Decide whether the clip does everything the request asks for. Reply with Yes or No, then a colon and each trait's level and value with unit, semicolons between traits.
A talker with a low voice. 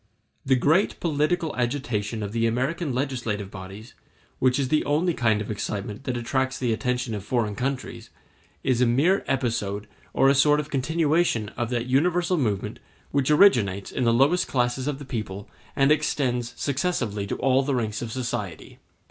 Yes: low, 125 Hz